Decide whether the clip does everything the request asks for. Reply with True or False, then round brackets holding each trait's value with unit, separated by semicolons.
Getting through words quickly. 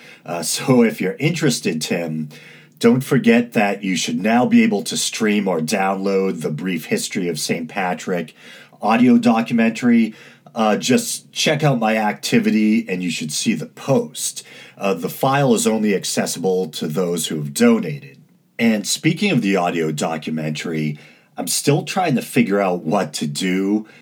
False (160 wpm)